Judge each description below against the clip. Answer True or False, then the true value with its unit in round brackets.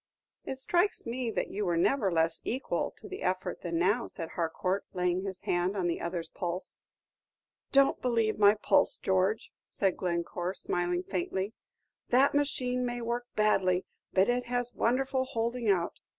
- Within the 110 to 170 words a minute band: True (160 wpm)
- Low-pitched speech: False (200 Hz)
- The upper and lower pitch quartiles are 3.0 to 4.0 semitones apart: False (5.4 semitones)